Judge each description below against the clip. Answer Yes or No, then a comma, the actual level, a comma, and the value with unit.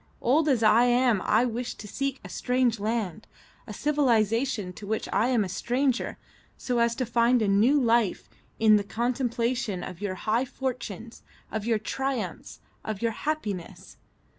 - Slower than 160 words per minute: No, average, 165 wpm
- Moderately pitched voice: No, high, 235 Hz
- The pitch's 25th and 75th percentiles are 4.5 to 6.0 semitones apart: No, average, 2.9 semitones